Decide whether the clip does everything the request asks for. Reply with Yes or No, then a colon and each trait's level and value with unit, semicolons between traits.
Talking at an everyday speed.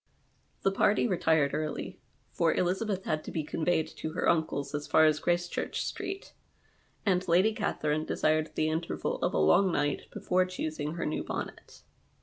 Yes: average, 160 wpm